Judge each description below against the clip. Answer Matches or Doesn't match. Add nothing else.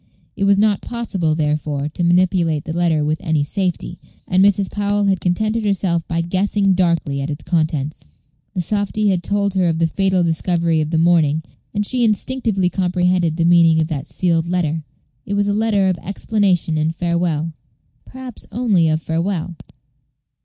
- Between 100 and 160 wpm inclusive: Doesn't match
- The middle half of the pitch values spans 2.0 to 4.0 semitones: Matches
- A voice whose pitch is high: Doesn't match